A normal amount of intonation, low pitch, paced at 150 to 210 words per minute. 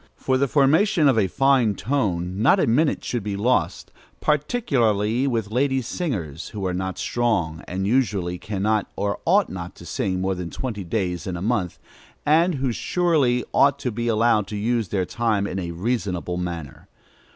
No: wide, 5.9 semitones; low, 110 Hz; average, 175 wpm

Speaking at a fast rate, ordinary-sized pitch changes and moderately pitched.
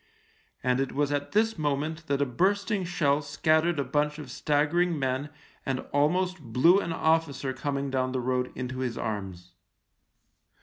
No: average, 160 wpm; average, 3.9 semitones; medium, 145 Hz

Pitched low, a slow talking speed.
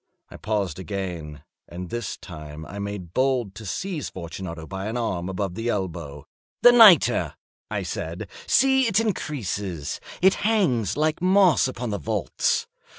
No: low, 100 Hz; average, 150 wpm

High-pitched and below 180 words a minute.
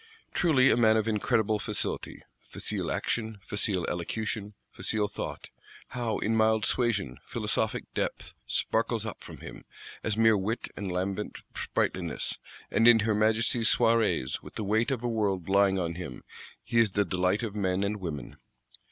No: low, 105 Hz; average, 160 wpm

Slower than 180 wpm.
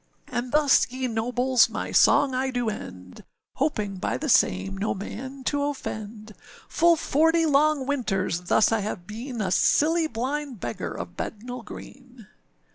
Yes: average, 150 wpm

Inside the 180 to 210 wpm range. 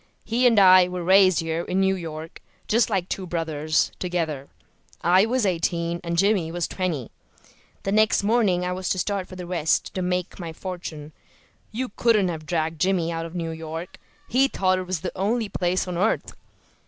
Yes: average, 190 wpm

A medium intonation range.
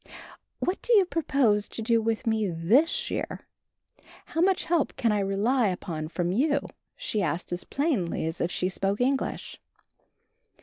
No: wide, 7.6 semitones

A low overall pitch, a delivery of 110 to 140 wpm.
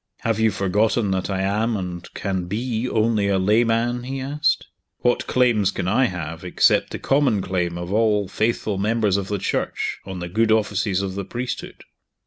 No: low, 105 Hz; average, 180 wpm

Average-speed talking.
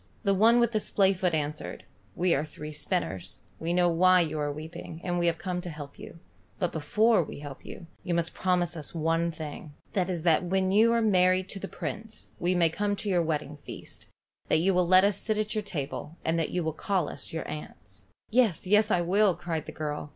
No: fast, 230 wpm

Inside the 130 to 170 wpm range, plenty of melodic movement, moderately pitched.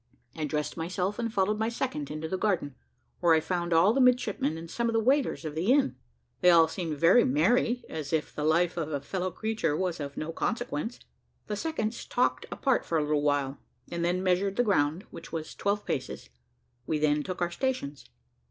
No: fast, 205 wpm; wide, 5.8 semitones; medium, 175 Hz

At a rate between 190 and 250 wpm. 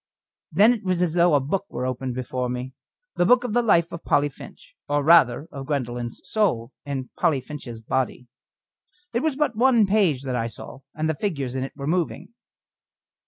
Yes: average, 195 wpm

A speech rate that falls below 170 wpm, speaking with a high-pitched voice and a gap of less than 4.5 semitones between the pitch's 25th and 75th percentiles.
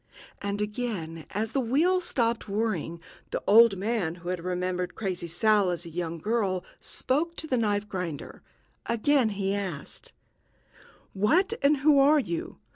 No: average, 150 wpm; high, 205 Hz; average, 4.9 semitones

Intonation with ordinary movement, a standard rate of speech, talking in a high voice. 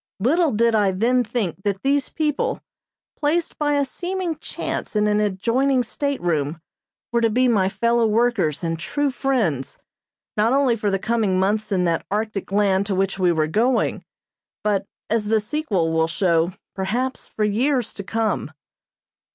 Yes: average, 5.0 semitones; average, 160 wpm; high, 215 Hz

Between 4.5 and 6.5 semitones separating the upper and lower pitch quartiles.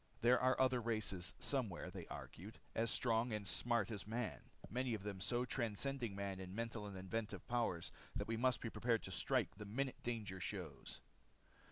No: average, 3.7 semitones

